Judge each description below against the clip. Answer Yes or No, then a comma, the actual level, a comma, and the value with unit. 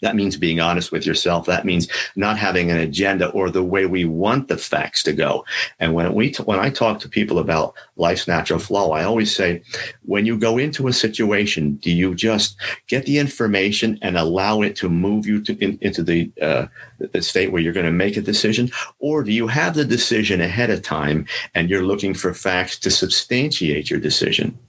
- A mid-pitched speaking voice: No, low, 100 Hz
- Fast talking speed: Yes, fast, 210 wpm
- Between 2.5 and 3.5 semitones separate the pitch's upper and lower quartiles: No, average, 4.1 semitones